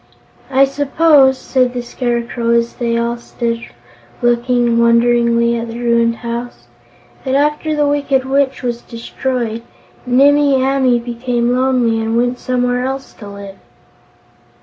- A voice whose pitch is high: Yes, high, 245 Hz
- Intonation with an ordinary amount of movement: No, narrow, 2.1 semitones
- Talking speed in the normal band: No, slow, 130 wpm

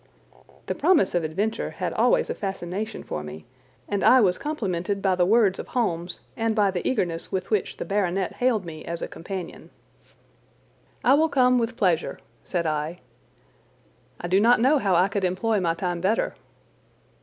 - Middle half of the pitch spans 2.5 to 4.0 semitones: No, average, 4.4 semitones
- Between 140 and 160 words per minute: No, average, 175 wpm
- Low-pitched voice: No, high, 195 Hz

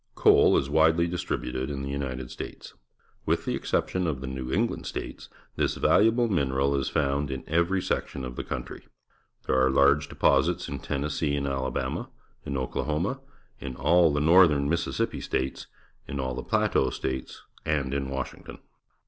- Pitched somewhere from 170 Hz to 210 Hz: No, very low, 70 Hz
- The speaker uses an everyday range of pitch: Yes, average, 3.5 semitones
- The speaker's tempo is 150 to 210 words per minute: Yes, average, 165 wpm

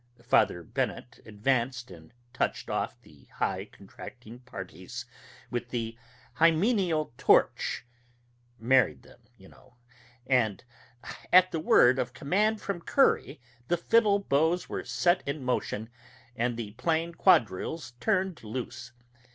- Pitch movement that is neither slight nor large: No, wide, 6.5 semitones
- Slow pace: Yes, slow, 120 wpm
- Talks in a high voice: No, low, 130 Hz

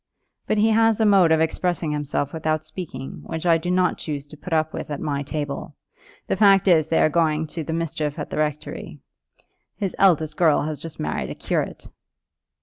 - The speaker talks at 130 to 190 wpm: No, average, 200 wpm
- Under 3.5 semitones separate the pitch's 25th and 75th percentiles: Yes, average, 3.0 semitones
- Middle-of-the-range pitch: Yes, medium, 160 Hz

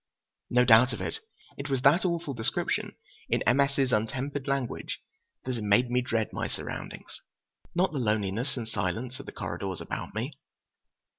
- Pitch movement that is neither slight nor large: Yes, average, 3.7 semitones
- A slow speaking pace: No, average, 165 wpm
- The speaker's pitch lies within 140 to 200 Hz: No, low, 125 Hz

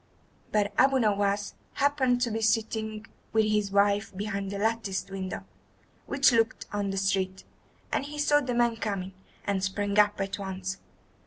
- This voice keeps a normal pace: Yes, average, 160 wpm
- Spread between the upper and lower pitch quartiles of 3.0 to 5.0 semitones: No, narrow, 2.5 semitones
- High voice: Yes, high, 205 Hz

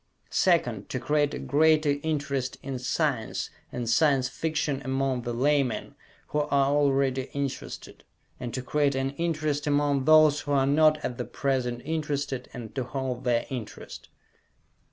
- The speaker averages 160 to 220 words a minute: No, average, 150 wpm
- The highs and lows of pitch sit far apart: No, narrow, 2.5 semitones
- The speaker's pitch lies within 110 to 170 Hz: Yes, medium, 140 Hz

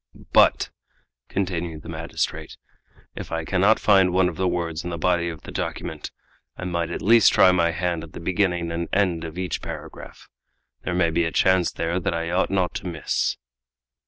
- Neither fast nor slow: Yes, average, 190 wpm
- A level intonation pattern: Yes, narrow, 1.9 semitones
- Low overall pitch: Yes, very low, 85 Hz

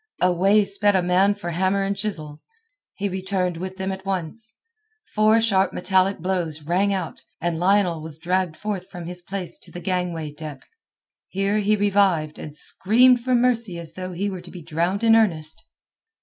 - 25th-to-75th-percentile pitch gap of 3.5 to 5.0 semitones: No, average, 2.7 semitones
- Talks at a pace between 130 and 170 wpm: No, average, 180 wpm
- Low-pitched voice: No, medium, 185 Hz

